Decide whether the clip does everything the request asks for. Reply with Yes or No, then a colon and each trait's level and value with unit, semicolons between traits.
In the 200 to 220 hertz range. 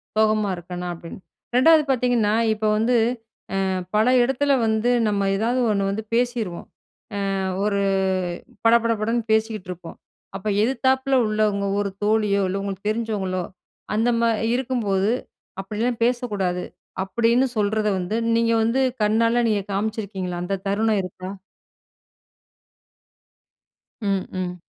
Yes: high, 215 Hz